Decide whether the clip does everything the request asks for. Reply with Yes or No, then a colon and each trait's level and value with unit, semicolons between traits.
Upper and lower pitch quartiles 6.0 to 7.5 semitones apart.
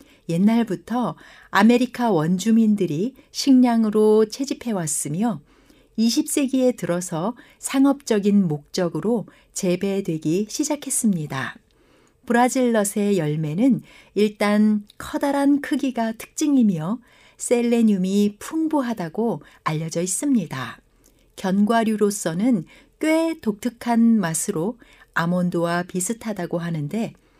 No: wide, 5.6 semitones